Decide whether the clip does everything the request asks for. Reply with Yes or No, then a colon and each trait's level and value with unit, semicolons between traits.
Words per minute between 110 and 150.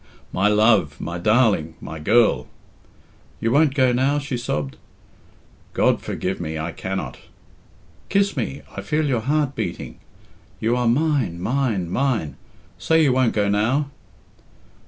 Yes: slow, 135 wpm